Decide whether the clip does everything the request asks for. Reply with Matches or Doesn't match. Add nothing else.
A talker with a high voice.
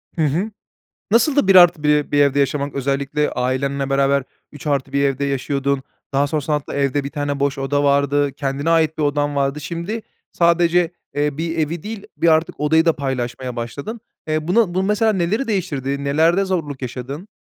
Doesn't match